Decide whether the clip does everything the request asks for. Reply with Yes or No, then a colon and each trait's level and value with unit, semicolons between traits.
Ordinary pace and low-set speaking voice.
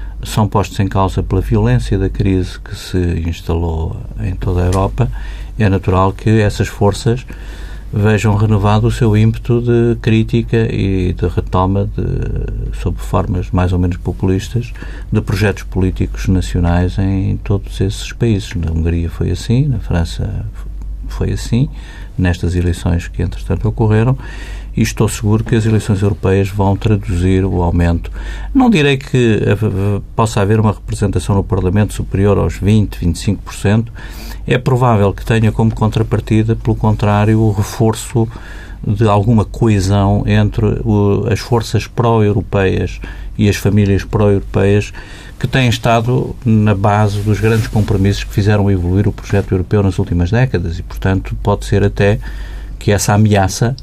Yes: average, 145 wpm; low, 100 Hz